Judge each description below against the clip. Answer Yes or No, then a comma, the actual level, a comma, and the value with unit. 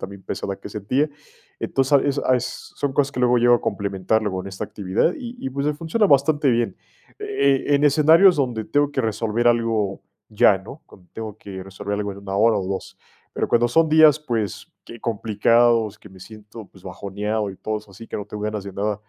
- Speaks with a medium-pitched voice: No, low, 115 Hz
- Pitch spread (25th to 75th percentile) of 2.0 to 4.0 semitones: No, average, 5.1 semitones